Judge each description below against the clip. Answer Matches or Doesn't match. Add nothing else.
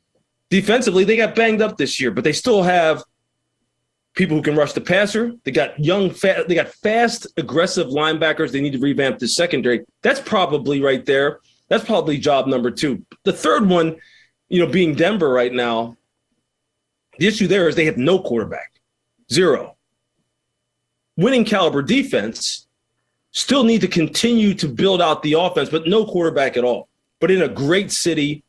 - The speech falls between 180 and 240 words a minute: Doesn't match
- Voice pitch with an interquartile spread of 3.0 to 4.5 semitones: Doesn't match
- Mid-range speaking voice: Matches